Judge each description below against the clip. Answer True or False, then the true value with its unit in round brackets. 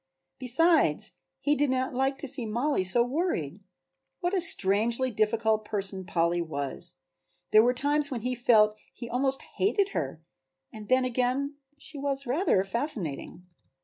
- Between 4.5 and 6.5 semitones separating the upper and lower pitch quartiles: True (4.9 semitones)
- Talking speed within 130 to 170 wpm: True (150 wpm)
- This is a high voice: True (245 Hz)